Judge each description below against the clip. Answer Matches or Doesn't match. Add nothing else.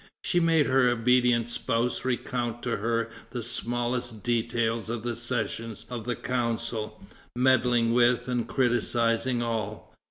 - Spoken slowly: Matches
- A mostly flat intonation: Matches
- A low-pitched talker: Matches